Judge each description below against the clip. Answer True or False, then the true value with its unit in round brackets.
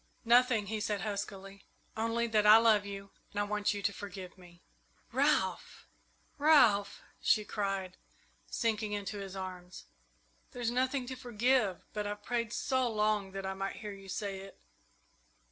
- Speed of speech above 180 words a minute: False (155 wpm)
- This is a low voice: False (205 Hz)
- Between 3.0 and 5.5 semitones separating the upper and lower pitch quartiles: False (2.6 semitones)